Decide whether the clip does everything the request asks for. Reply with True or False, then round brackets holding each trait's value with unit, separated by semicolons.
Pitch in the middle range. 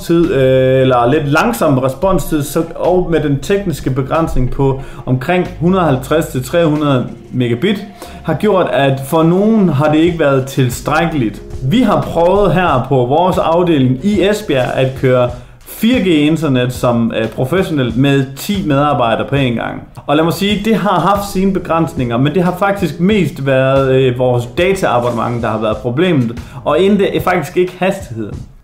True (150 Hz)